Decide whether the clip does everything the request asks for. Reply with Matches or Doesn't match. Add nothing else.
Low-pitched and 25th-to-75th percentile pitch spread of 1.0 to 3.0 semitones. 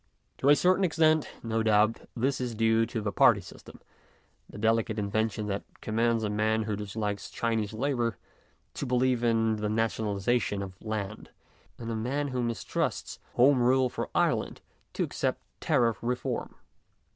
Matches